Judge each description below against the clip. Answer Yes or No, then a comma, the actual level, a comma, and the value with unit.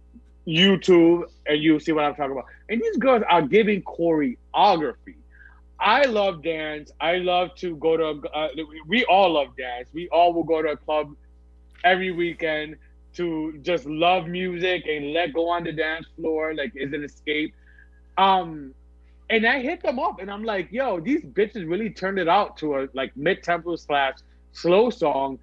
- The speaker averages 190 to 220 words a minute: No, average, 175 wpm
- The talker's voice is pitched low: No, medium, 165 Hz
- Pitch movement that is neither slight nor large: Yes, average, 4.0 semitones